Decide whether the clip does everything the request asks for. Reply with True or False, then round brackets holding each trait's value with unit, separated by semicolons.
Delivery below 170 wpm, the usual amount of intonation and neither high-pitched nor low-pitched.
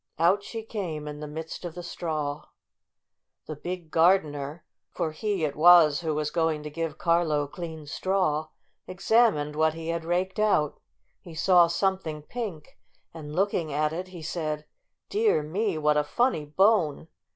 True (160 wpm; 3.4 semitones; 160 Hz)